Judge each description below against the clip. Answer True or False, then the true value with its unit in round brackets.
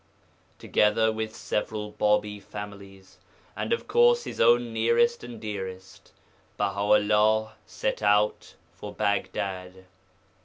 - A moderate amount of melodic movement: False (1.7 semitones)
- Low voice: True (105 Hz)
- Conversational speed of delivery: False (110 wpm)